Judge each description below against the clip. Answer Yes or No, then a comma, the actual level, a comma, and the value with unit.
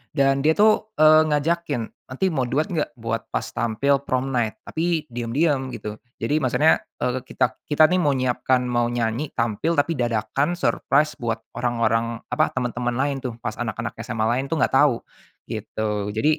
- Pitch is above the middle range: No, low, 130 Hz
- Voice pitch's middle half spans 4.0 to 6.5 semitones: Yes, average, 4.3 semitones